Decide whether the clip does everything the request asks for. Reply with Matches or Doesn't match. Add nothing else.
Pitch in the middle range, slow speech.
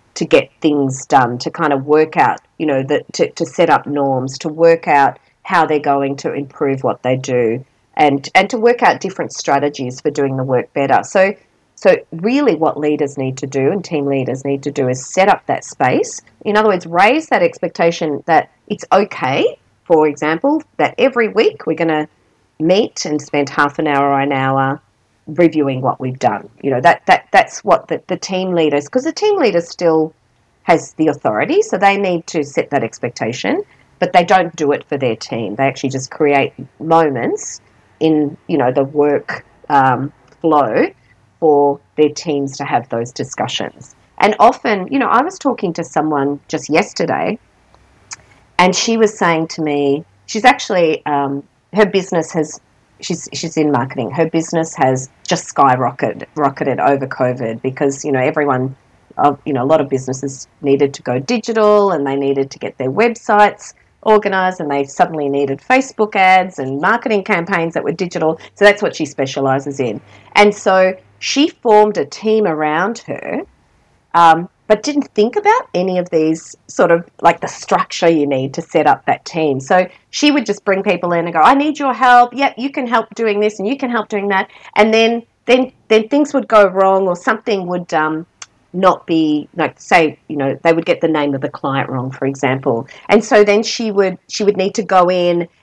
Doesn't match